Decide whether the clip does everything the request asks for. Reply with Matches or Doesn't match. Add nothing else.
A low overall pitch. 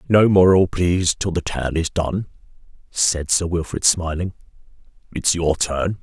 Matches